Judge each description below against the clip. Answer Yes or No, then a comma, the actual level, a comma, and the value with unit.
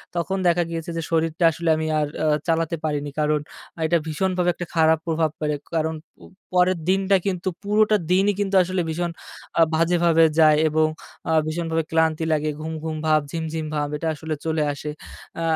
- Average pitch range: No, narrow, 2.0 semitones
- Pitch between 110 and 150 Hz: No, medium, 165 Hz